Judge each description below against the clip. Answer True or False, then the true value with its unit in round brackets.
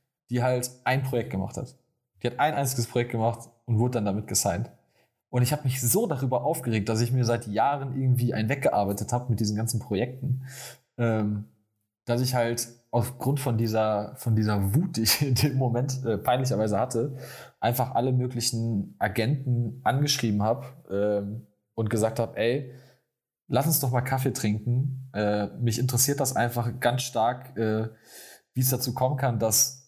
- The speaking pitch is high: False (120 Hz)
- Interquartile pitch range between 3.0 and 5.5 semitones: False (2.6 semitones)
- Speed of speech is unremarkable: True (175 wpm)